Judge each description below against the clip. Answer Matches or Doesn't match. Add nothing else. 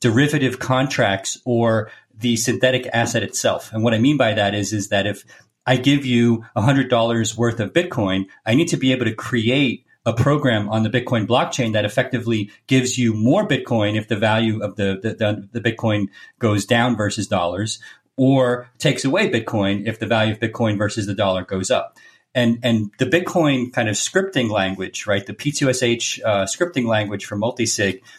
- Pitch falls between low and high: Doesn't match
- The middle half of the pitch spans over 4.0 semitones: Doesn't match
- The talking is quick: Doesn't match